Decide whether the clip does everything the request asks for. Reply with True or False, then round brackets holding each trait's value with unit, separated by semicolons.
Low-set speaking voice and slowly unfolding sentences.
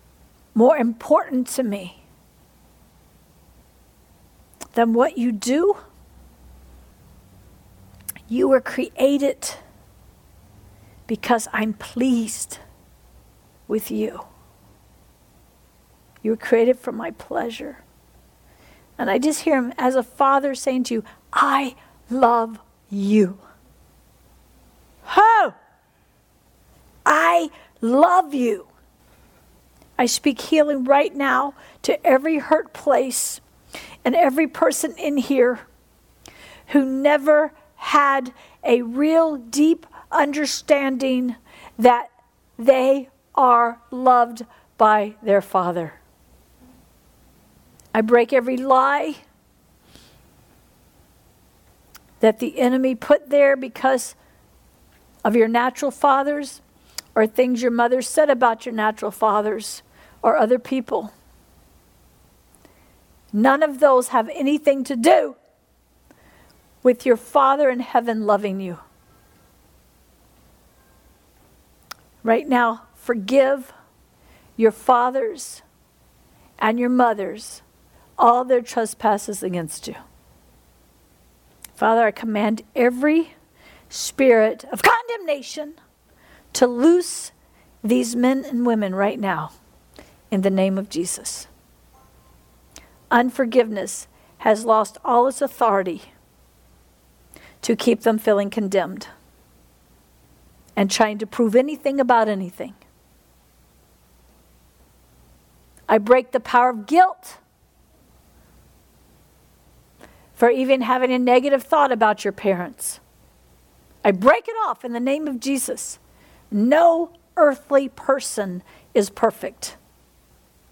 False (235 Hz; 95 wpm)